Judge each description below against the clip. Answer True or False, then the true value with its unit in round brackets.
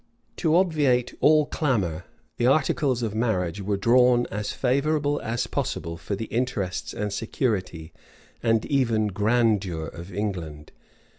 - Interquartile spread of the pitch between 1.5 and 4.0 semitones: False (4.9 semitones)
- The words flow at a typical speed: False (130 wpm)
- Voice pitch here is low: True (110 Hz)